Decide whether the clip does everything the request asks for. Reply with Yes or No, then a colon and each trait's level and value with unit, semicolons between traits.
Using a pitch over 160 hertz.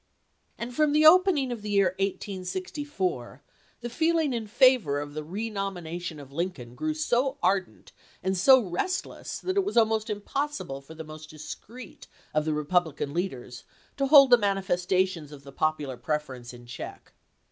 Yes: high, 190 Hz